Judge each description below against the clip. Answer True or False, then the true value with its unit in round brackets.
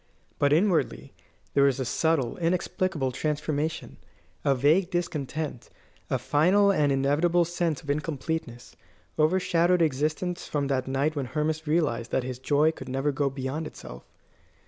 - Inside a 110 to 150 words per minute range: True (140 wpm)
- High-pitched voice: False (150 Hz)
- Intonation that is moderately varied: True (3.5 semitones)